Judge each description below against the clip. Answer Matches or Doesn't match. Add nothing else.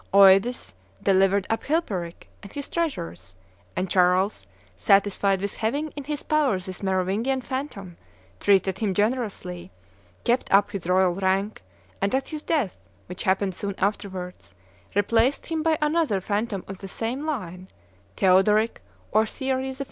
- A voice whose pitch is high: Matches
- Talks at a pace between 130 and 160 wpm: Matches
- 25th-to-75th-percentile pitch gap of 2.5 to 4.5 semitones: Doesn't match